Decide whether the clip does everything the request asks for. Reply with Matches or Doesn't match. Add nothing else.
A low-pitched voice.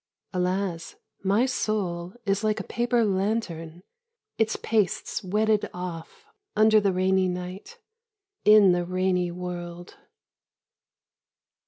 Doesn't match